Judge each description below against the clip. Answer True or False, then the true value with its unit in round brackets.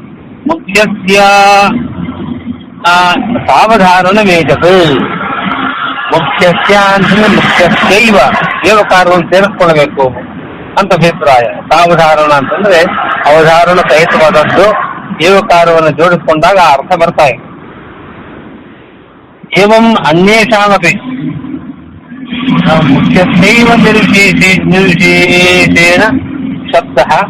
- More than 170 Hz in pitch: True (185 Hz)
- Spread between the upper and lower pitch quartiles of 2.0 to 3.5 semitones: False (3.9 semitones)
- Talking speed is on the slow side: True (55 wpm)